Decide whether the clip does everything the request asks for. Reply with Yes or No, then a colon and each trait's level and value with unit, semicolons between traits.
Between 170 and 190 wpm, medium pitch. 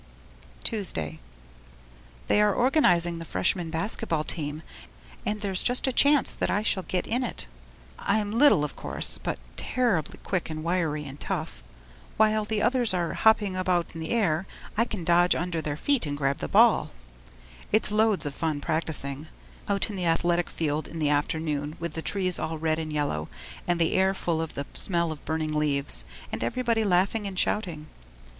Yes: average, 180 wpm; medium, 175 Hz